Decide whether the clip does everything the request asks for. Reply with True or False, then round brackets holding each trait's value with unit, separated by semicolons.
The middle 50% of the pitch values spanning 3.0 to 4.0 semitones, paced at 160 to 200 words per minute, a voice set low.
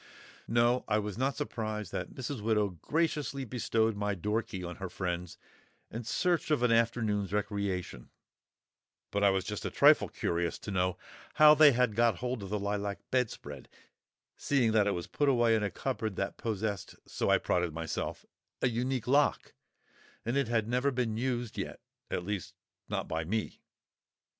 True (3.6 semitones; 165 wpm; 110 Hz)